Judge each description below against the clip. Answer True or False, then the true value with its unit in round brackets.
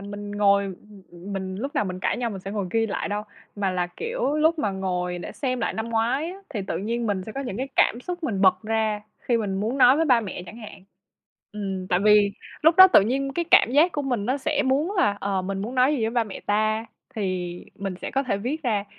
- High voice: True (215 Hz)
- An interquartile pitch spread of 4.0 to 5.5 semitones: True (5.0 semitones)